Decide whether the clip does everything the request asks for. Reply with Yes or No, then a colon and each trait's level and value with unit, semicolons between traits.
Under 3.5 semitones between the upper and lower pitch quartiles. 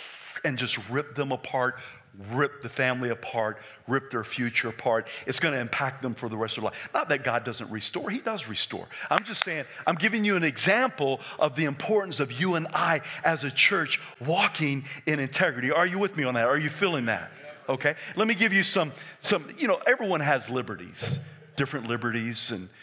No: average, 4.6 semitones